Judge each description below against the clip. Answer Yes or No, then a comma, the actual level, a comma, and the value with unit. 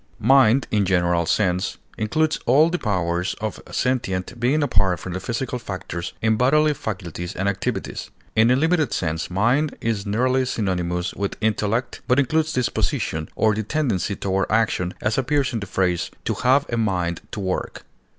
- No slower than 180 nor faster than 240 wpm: No, average, 170 wpm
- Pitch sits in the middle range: No, low, 110 Hz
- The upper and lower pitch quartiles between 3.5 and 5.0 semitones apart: No, wide, 5.5 semitones